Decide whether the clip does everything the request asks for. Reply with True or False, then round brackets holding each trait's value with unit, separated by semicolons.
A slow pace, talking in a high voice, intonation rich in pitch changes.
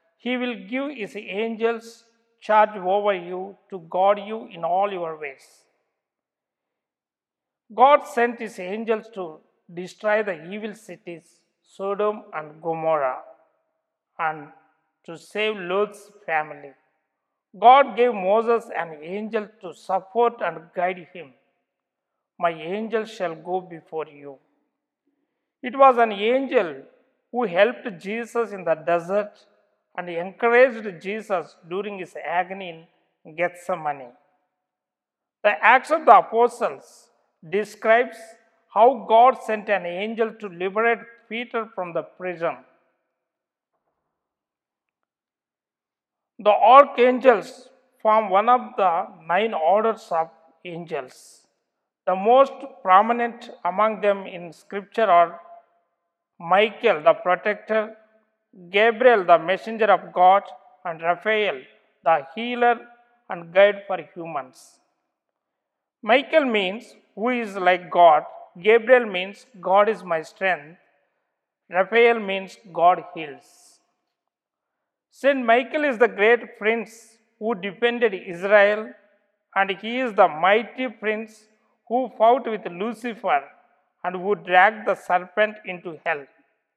False (110 wpm; 205 Hz; 4.6 semitones)